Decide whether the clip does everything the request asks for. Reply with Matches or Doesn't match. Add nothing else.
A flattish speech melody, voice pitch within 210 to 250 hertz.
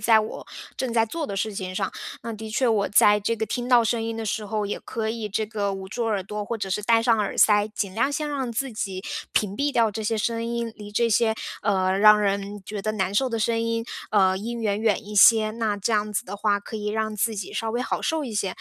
Matches